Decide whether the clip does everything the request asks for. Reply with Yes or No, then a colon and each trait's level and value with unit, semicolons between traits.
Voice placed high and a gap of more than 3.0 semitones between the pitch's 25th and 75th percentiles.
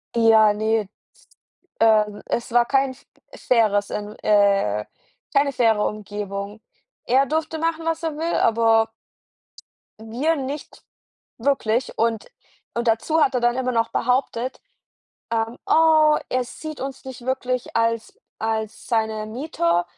Yes: high, 230 Hz; average, 3.7 semitones